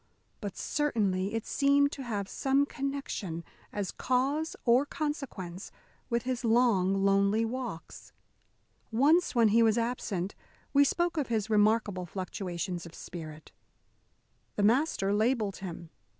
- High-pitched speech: Yes, high, 225 Hz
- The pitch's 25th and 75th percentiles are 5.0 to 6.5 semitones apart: Yes, wide, 5.5 semitones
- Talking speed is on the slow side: Yes, slow, 125 wpm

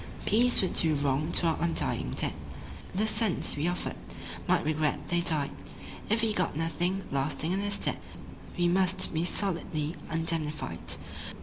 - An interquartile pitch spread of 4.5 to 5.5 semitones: No, average, 3.6 semitones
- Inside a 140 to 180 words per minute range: Yes, average, 150 wpm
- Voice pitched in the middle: Yes, medium, 170 Hz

